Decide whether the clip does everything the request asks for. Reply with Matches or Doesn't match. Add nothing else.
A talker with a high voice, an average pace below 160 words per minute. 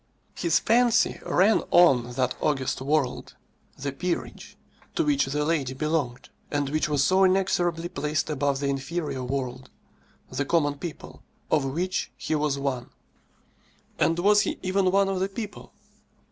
Doesn't match